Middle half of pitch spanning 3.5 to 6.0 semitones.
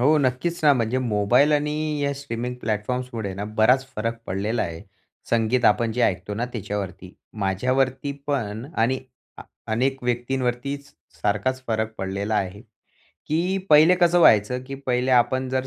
Yes: average, 3.9 semitones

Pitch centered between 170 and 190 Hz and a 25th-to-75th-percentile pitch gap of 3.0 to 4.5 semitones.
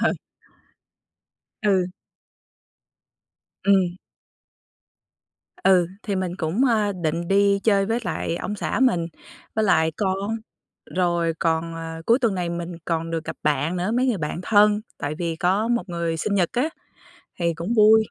Yes: medium, 185 Hz; average, 3.8 semitones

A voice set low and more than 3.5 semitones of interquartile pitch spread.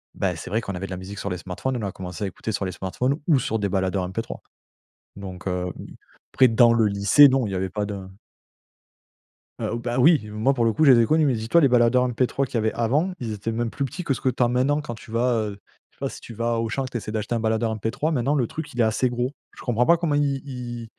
Yes: low, 115 Hz; average, 3.9 semitones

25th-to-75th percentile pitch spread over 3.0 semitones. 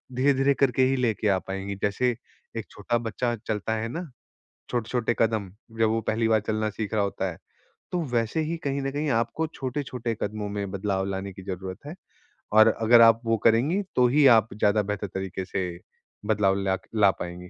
Yes: average, 3.6 semitones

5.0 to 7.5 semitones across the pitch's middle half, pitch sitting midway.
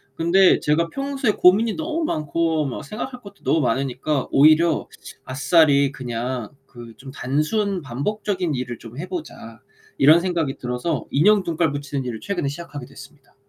Yes: average, 5.3 semitones; medium, 150 Hz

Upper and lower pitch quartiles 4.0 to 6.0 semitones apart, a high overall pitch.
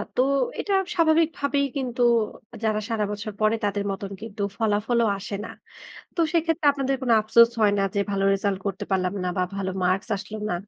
Yes: average, 4.7 semitones; high, 215 Hz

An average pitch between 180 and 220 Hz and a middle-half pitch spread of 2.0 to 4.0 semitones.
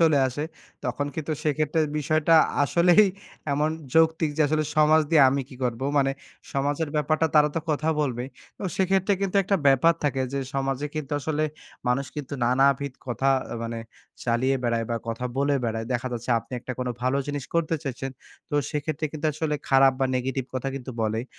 No: medium, 140 Hz; average, 3.2 semitones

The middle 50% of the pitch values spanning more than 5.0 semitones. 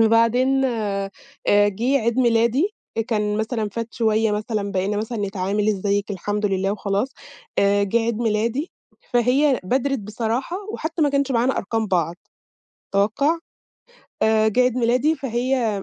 No: average, 3.4 semitones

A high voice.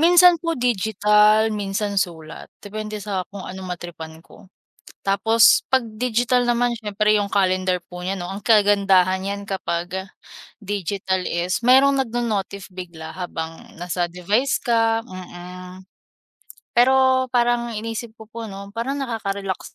Yes: high, 205 Hz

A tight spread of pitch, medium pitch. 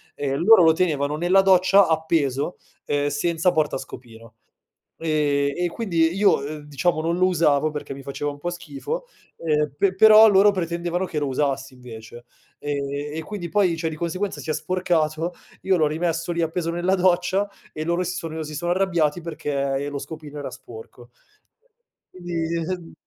No: average, 3.5 semitones; medium, 160 Hz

